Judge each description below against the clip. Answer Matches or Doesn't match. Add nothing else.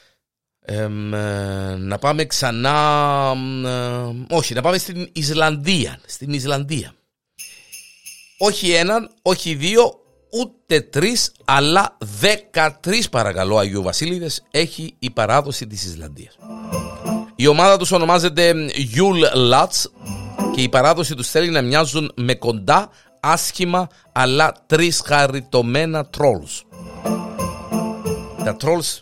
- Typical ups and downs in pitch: Doesn't match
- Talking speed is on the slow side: Matches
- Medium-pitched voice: Matches